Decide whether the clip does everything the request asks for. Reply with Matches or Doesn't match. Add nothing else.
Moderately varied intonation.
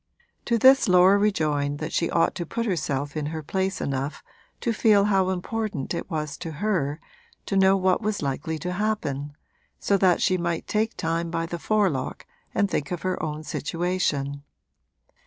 Matches